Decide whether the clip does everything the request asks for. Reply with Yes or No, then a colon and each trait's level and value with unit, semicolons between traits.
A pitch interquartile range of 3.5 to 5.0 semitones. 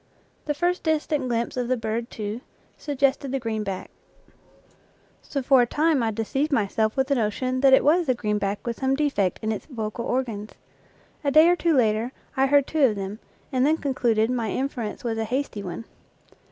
Yes: average, 4.2 semitones